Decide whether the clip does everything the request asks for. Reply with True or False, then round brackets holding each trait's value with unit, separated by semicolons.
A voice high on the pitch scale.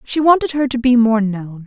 True (245 Hz)